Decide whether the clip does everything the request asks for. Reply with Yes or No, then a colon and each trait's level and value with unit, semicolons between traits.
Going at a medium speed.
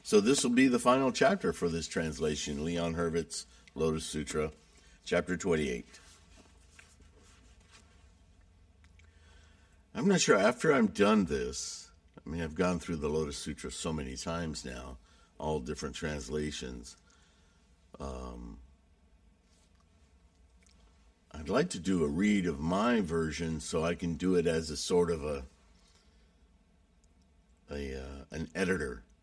No: slow, 130 wpm